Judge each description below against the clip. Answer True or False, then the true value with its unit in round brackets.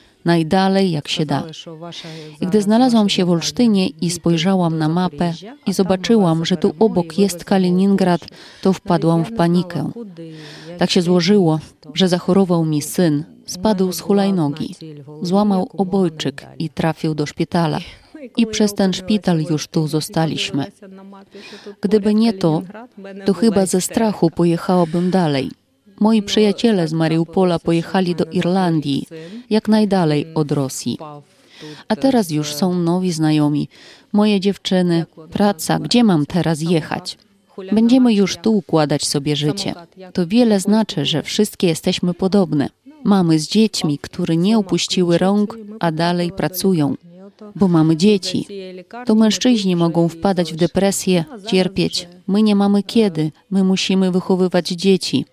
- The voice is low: False (185 Hz)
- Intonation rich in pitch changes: False (3.5 semitones)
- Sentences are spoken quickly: False (130 wpm)